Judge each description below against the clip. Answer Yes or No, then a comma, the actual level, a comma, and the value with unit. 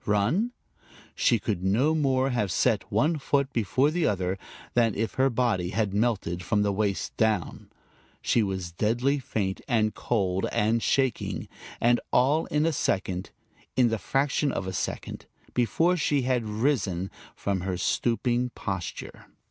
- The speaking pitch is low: Yes, low, 115 Hz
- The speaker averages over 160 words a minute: No, average, 150 wpm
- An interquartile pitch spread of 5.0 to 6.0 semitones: Yes, average, 5.3 semitones